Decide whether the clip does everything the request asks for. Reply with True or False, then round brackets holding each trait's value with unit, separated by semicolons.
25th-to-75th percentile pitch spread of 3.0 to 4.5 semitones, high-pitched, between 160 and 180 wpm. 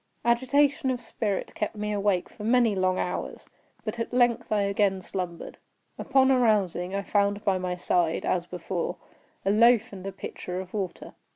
True (4.0 semitones; 205 Hz; 170 wpm)